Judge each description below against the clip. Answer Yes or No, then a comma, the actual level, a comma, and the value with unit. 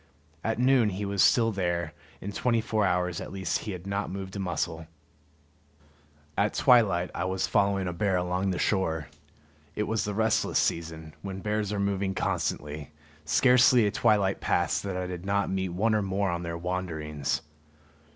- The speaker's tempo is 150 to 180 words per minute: Yes, average, 175 wpm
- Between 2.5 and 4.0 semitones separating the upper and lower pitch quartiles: Yes, average, 2.9 semitones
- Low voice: Yes, very low, 95 Hz